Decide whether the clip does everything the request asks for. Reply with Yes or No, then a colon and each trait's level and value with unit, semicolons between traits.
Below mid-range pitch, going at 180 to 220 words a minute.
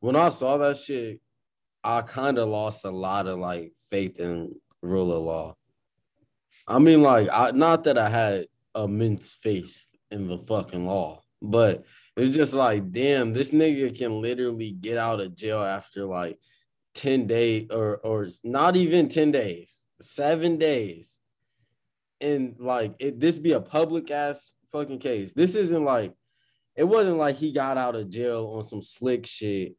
No: low, 115 Hz; average, 165 wpm